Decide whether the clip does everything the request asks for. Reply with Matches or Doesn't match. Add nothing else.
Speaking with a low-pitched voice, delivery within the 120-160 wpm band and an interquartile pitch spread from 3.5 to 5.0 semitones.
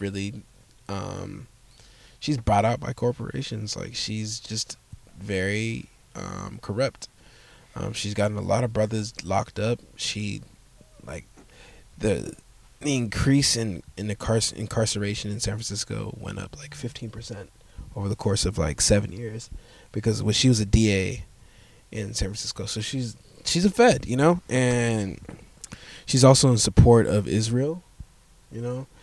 Doesn't match